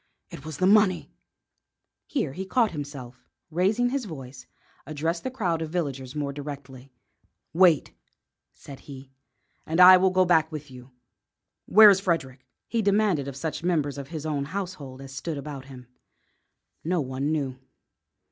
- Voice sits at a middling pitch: Yes, medium, 155 Hz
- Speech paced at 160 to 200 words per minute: Yes, average, 165 wpm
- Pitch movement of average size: Yes, average, 5.0 semitones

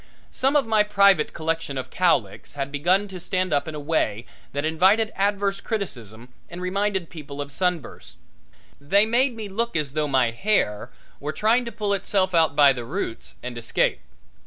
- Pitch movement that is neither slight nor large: No, wide, 6.2 semitones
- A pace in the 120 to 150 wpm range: No, average, 180 wpm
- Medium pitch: Yes, medium, 175 Hz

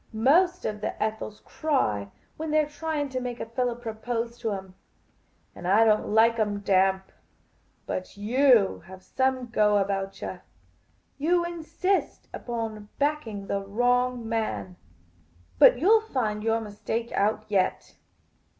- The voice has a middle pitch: No, high, 225 Hz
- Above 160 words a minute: No, average, 140 wpm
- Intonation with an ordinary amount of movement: Yes, average, 4.2 semitones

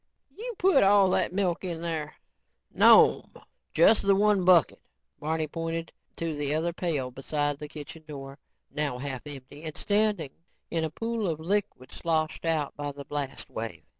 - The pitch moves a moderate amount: Yes, average, 4.0 semitones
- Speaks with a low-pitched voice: No, medium, 160 Hz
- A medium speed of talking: Yes, average, 165 wpm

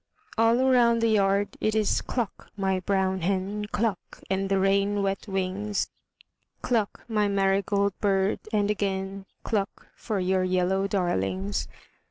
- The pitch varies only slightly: Yes, narrow, 1.5 semitones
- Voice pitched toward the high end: Yes, high, 195 Hz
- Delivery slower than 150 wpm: Yes, slow, 135 wpm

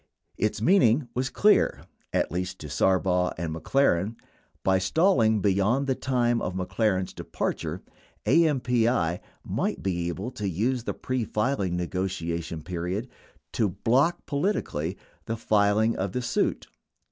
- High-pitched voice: No, low, 105 Hz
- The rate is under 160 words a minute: Yes, average, 140 wpm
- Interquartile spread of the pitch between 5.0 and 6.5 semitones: Yes, wide, 5.6 semitones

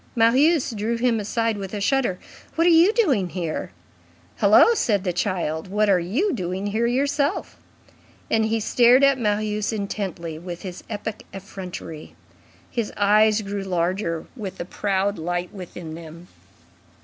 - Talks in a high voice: Yes, high, 205 Hz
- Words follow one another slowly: No, average, 150 wpm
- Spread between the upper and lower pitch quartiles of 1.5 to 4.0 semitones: No, average, 4.4 semitones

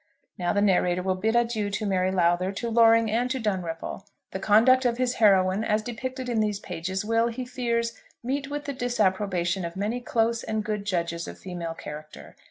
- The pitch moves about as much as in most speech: Yes, average, 4.1 semitones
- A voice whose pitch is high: Yes, high, 210 Hz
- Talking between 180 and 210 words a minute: Yes, average, 190 wpm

